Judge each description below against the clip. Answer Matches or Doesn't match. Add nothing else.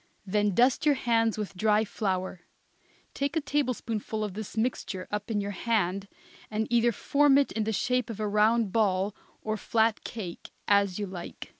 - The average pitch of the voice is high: Matches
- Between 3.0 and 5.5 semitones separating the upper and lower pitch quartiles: Doesn't match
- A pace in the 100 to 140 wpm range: Doesn't match